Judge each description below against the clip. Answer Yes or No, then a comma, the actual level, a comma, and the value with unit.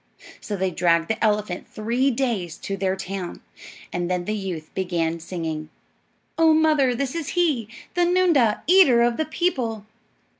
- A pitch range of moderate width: No, wide, 7.5 semitones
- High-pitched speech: Yes, high, 215 Hz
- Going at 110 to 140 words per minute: No, average, 155 wpm